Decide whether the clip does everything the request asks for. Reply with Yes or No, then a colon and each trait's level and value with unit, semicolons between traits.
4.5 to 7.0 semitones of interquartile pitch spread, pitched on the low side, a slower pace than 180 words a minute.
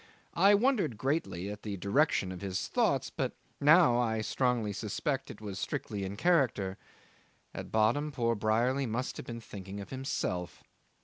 Yes: average, 5.0 semitones; low, 115 Hz; average, 160 wpm